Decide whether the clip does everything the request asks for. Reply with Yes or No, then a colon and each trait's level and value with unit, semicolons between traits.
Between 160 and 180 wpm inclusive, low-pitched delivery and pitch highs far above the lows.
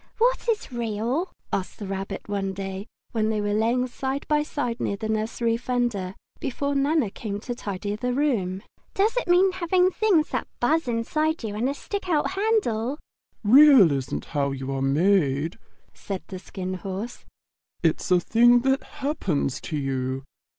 No: average, 165 wpm; high, 230 Hz; wide, 6.9 semitones